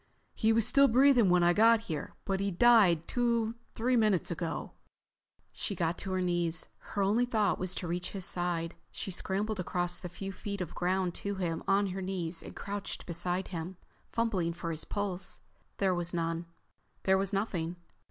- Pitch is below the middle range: No, high, 190 Hz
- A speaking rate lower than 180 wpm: No, average, 185 wpm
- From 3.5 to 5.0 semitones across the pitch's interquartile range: No, average, 2.9 semitones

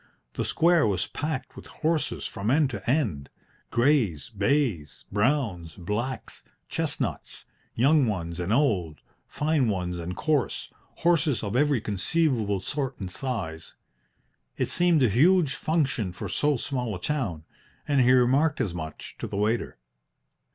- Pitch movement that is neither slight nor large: No, wide, 7.5 semitones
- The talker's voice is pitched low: Yes, low, 120 Hz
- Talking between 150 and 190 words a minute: No, average, 140 wpm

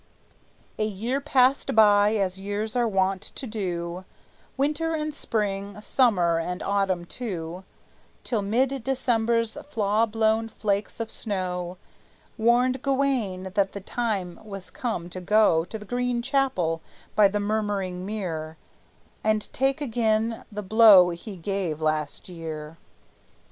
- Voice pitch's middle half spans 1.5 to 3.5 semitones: No, average, 4.0 semitones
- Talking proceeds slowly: Yes, slow, 130 wpm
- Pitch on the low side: No, high, 210 Hz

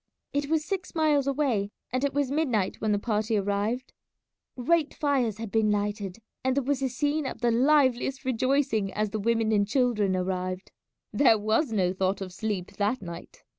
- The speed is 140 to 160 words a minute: No, average, 180 wpm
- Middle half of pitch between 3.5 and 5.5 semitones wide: Yes, average, 5.2 semitones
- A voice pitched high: Yes, high, 230 Hz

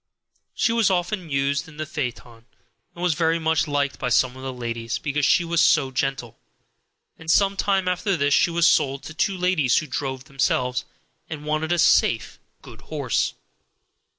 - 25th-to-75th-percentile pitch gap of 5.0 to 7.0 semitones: No, average, 4.3 semitones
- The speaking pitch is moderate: Yes, medium, 150 Hz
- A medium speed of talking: Yes, average, 180 wpm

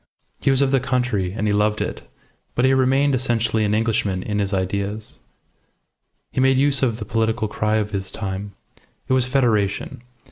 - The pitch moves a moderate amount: Yes, average, 3.9 semitones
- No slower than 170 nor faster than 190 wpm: Yes, average, 180 wpm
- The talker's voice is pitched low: Yes, low, 110 Hz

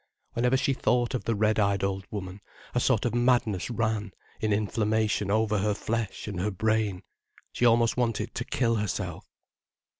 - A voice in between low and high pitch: No, low, 110 Hz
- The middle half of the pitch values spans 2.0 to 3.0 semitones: Yes, narrow, 2.4 semitones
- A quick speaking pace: No, average, 170 wpm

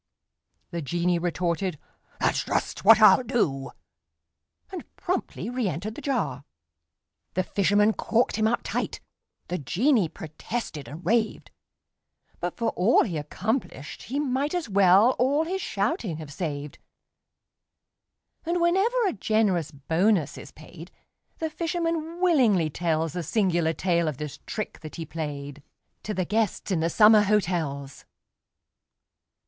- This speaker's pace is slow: Yes, slow, 130 wpm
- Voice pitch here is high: Yes, high, 195 Hz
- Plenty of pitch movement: Yes, wide, 6.8 semitones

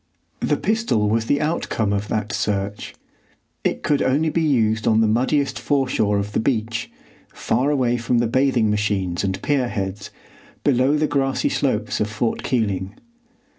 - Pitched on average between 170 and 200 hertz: No, low, 115 Hz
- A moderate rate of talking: Yes, average, 155 wpm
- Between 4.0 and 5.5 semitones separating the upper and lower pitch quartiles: Yes, average, 4.6 semitones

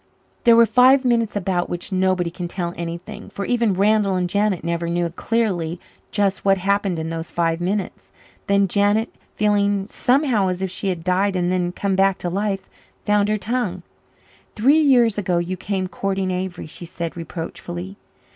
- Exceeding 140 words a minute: Yes, average, 175 wpm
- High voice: Yes, high, 195 Hz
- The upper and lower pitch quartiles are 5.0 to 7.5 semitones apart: No, average, 2.9 semitones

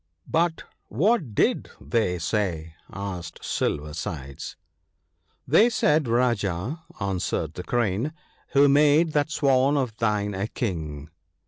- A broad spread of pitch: Yes, wide, 8.6 semitones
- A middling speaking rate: No, slow, 125 wpm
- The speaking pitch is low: Yes, low, 105 Hz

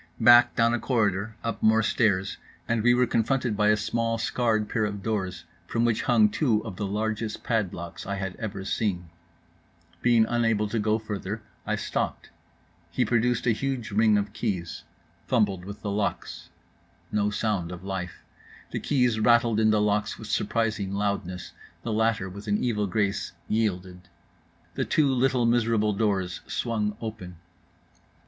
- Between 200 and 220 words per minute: No, average, 155 wpm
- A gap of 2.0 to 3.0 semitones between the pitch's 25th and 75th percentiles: Yes, narrow, 2.4 semitones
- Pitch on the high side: No, low, 110 Hz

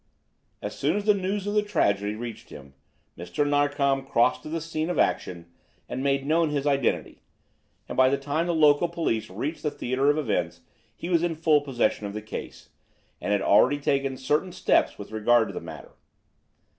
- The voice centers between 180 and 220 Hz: No, medium, 140 Hz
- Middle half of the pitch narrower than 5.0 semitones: No, wide, 5.4 semitones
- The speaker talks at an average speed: Yes, average, 195 wpm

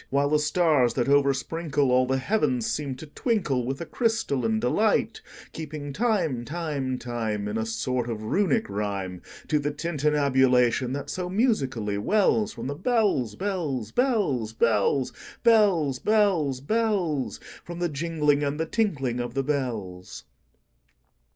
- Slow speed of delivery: Yes, slow, 120 wpm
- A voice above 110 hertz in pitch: Yes, medium, 140 Hz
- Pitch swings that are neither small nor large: No, wide, 5.8 semitones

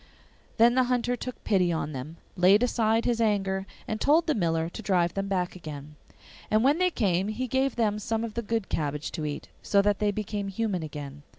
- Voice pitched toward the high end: Yes, high, 205 Hz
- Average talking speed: No, fast, 210 wpm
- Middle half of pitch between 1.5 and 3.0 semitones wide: No, average, 4.9 semitones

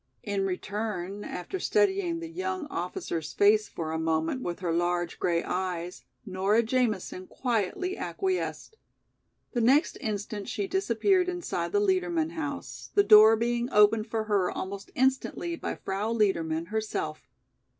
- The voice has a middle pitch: No, high, 215 Hz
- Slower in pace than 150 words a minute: Yes, average, 140 wpm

